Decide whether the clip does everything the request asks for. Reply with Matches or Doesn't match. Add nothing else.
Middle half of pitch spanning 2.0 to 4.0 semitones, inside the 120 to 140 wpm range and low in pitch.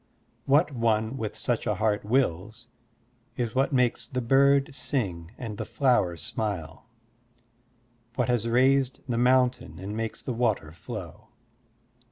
Matches